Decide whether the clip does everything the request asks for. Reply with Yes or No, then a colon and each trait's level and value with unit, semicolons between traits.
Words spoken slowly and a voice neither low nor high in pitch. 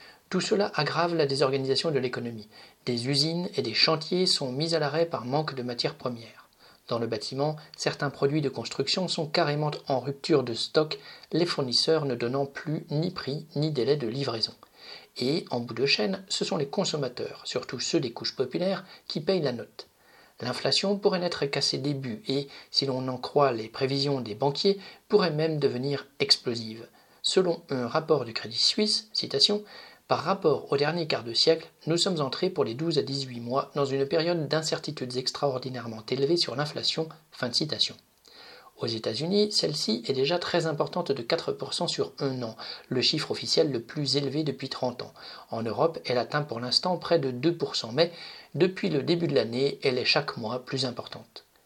No: average, 185 wpm; medium, 145 Hz